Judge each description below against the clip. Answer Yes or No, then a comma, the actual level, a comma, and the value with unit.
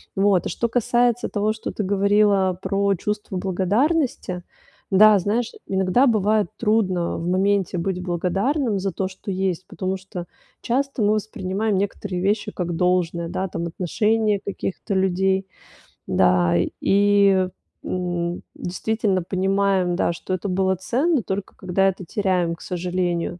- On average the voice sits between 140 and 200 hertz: Yes, high, 190 Hz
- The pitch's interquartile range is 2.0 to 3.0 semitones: Yes, narrow, 2.5 semitones